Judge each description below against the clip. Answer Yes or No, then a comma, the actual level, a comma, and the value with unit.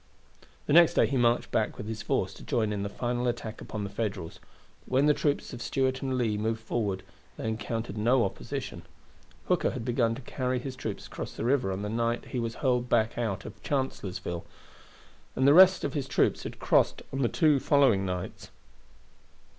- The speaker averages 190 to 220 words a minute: Yes, average, 200 wpm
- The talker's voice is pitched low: Yes, low, 120 Hz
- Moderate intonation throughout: Yes, average, 3.7 semitones